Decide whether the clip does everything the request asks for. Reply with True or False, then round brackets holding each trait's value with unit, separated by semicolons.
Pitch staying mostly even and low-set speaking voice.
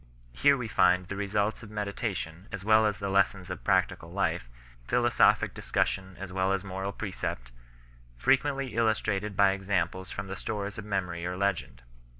True (2.3 semitones; 100 Hz)